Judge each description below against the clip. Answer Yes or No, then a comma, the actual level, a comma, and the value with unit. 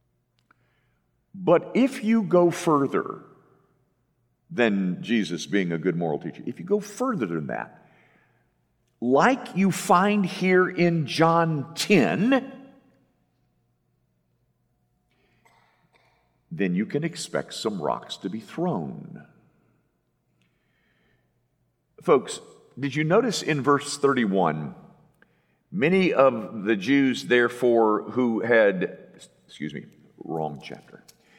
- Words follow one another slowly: Yes, slow, 100 wpm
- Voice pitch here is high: No, medium, 150 Hz